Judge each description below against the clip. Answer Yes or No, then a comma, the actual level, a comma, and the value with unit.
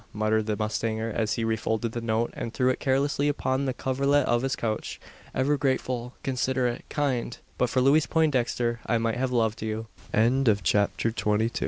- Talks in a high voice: No, low, 120 Hz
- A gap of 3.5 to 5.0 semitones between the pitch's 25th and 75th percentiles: No, average, 2.9 semitones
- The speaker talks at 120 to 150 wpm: No, average, 175 wpm